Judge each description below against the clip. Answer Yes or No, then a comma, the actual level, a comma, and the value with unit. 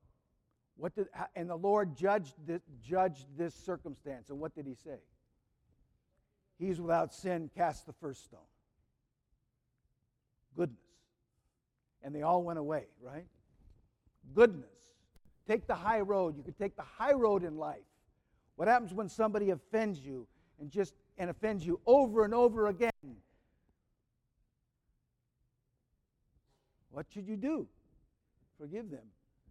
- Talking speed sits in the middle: No, slow, 130 wpm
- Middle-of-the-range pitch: Yes, medium, 170 Hz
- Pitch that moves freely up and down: Yes, wide, 6.6 semitones